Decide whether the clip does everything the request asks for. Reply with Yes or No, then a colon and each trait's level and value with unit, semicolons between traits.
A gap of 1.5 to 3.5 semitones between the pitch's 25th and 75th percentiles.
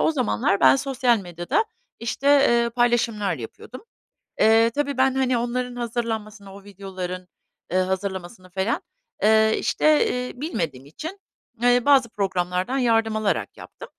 No: average, 4.6 semitones